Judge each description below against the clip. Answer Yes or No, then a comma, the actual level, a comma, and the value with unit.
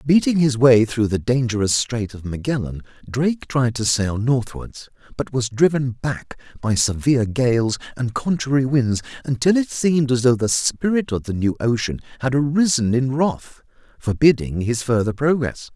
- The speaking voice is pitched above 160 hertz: No, low, 125 Hz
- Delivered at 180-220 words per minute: No, average, 165 wpm